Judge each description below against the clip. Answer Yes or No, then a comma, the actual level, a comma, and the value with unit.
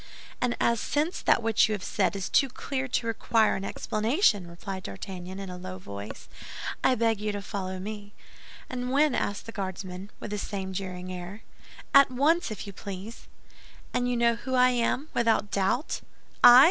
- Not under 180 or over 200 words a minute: Yes, average, 185 wpm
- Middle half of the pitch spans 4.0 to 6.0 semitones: Yes, average, 4.5 semitones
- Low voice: No, high, 210 Hz